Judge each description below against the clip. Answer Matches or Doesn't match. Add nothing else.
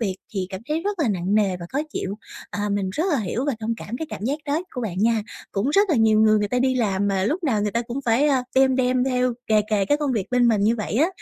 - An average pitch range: Matches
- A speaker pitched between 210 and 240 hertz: Matches